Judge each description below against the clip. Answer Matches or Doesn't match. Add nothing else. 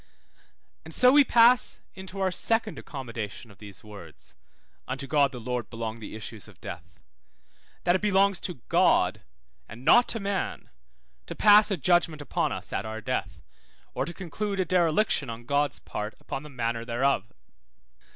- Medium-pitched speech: Matches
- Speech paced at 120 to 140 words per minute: Doesn't match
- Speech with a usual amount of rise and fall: Doesn't match